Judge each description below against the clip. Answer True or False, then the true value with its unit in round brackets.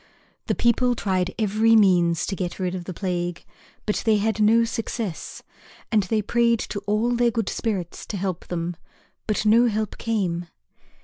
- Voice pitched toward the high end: True (210 Hz)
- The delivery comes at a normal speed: True (170 wpm)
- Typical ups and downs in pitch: True (3.8 semitones)